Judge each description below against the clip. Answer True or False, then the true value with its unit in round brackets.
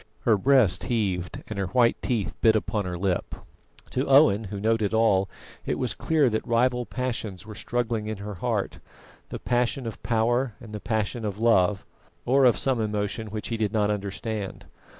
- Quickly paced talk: False (180 wpm)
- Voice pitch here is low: True (110 Hz)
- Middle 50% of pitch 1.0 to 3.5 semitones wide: True (2.9 semitones)